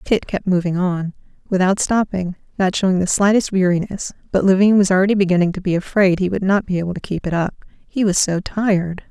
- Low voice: No, high, 190 Hz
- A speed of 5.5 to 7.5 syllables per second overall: Yes, 5.9 syllables/s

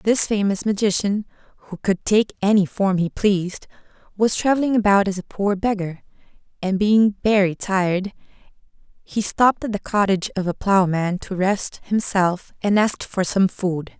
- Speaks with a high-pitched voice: Yes, high, 200 Hz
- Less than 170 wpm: Yes, average, 160 wpm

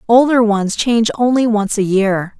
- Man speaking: No, female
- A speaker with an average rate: Yes, average, 175 wpm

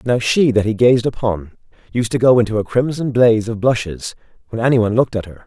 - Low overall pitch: Yes, low, 115 Hz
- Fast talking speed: Yes, fast, 230 wpm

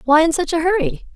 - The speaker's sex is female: Yes, female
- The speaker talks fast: Yes, fast, 260 wpm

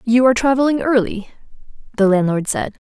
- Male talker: No, female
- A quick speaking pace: No, average, 145 wpm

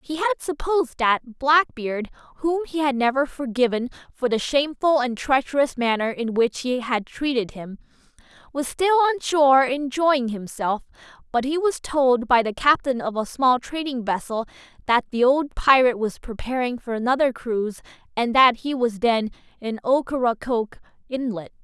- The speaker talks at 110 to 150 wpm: No, average, 160 wpm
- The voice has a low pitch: No, very high, 260 Hz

